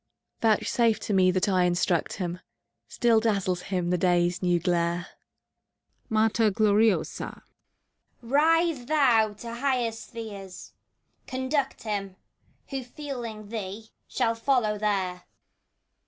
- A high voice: Yes, high, 215 Hz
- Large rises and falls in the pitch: No, average, 4.3 semitones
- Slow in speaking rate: Yes, slow, 110 wpm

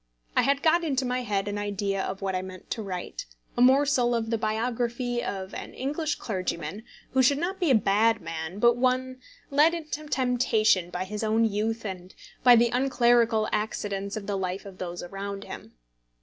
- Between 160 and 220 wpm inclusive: Yes, average, 190 wpm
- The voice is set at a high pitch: Yes, high, 225 Hz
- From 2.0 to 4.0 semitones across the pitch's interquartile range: No, average, 4.4 semitones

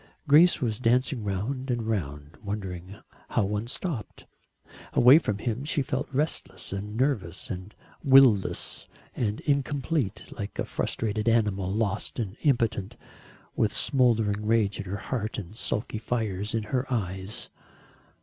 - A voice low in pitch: Yes, low, 110 Hz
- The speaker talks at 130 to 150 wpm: Yes, average, 140 wpm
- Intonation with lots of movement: No, average, 4.1 semitones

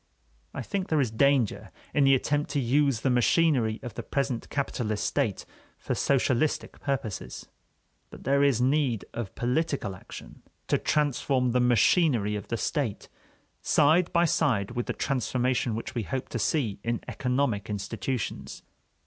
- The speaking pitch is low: Yes, low, 125 Hz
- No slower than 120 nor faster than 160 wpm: Yes, average, 150 wpm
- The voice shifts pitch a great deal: No, average, 3.7 semitones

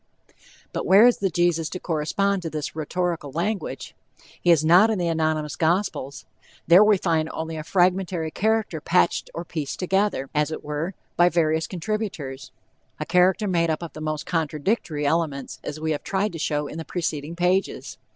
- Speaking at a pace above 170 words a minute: Yes, average, 180 wpm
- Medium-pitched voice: Yes, medium, 165 Hz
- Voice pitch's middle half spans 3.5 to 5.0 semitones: No, average, 3.0 semitones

